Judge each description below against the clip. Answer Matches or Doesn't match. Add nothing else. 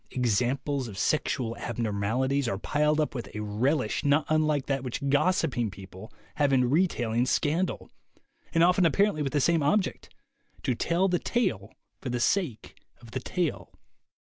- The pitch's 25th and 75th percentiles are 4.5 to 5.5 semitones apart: Matches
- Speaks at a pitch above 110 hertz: Matches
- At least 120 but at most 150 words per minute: Doesn't match